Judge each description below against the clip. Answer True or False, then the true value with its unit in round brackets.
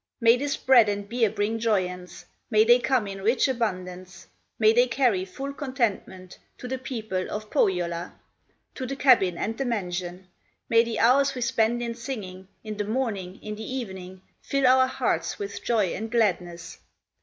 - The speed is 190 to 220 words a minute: False (170 wpm)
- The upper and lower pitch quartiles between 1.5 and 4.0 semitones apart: False (4.8 semitones)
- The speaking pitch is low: False (220 Hz)